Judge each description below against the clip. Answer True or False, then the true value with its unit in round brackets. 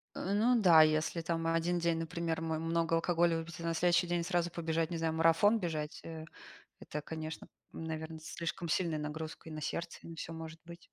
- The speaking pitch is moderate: True (165 Hz)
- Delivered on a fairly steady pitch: True (1.1 semitones)